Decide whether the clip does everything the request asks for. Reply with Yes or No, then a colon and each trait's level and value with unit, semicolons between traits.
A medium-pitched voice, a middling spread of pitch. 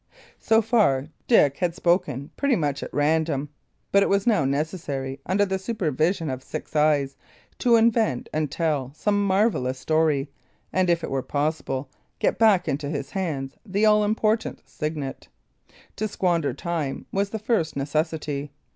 No: medium, 160 Hz; wide, 6.0 semitones